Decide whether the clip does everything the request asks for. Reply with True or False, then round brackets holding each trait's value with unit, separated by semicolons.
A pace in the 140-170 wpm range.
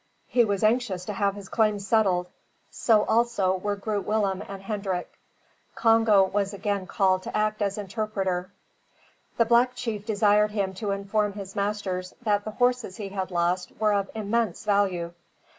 True (160 wpm)